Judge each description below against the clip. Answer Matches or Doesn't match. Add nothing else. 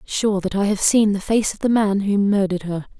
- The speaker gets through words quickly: Matches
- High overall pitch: Matches